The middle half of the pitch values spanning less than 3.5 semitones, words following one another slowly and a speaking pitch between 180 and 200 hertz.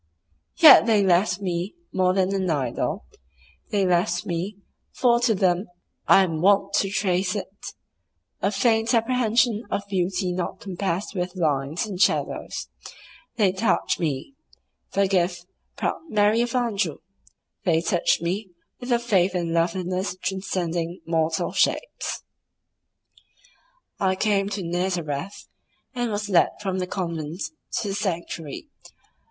Yes: average, 2.9 semitones; slow, 125 wpm; high, 190 Hz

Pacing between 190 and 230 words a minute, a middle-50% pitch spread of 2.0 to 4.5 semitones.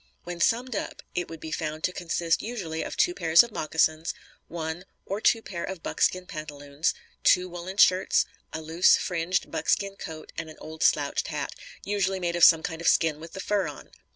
Yes: average, 195 wpm; average, 2.9 semitones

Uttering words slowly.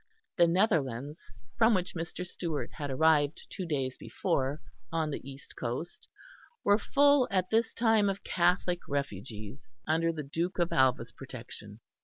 No: average, 145 wpm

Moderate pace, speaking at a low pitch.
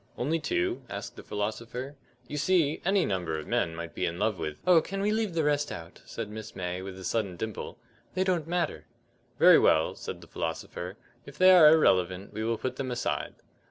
No: fast, 215 wpm; low, 115 Hz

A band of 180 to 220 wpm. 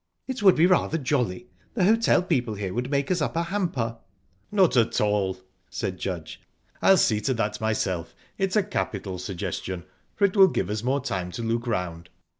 Yes: average, 190 wpm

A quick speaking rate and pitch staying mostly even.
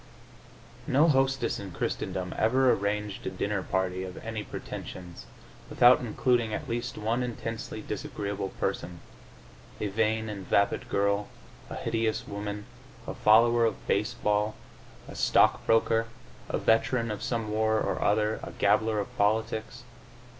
No: slow, 135 wpm; narrow, 2.2 semitones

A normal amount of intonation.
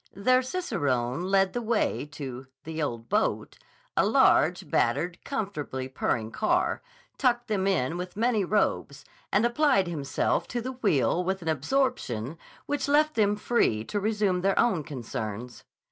No: wide, 8.8 semitones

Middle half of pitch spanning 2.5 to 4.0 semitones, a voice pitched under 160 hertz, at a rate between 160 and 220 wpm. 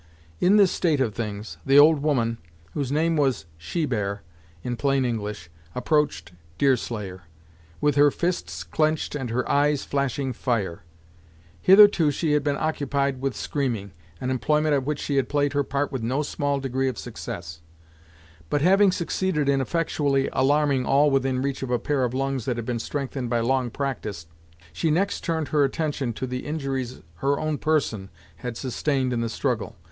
Yes: average, 3.3 semitones; low, 135 Hz; average, 170 wpm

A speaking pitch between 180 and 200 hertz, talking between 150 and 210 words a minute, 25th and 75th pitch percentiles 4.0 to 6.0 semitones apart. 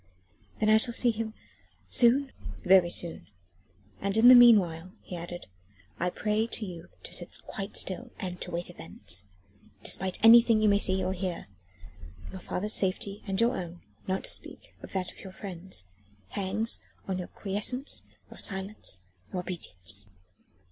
No: high, 190 Hz; average, 155 wpm; average, 3.4 semitones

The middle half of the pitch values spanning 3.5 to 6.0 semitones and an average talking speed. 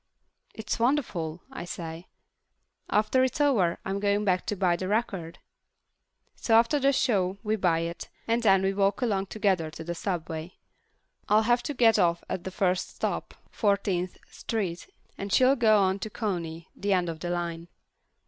Yes: average, 4.0 semitones; average, 170 wpm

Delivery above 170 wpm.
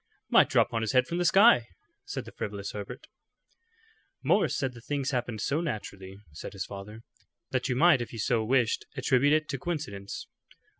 Yes: average, 185 wpm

